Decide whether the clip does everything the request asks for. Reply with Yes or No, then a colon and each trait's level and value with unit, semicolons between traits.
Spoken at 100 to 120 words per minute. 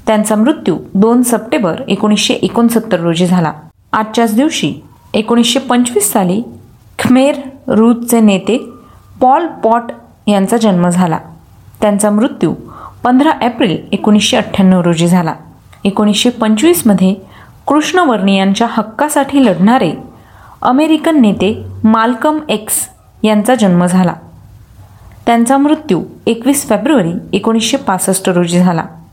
Yes: average, 105 wpm